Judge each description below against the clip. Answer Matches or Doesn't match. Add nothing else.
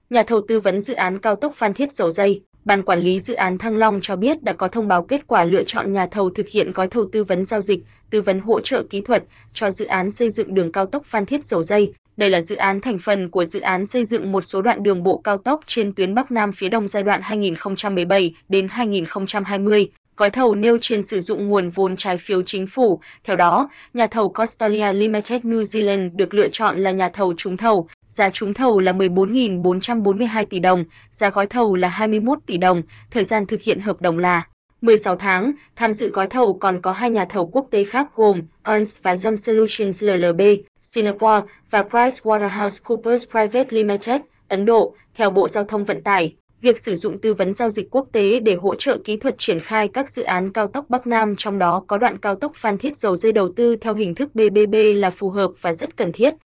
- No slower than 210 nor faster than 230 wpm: Matches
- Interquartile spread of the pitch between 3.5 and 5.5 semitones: Doesn't match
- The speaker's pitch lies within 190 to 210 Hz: Matches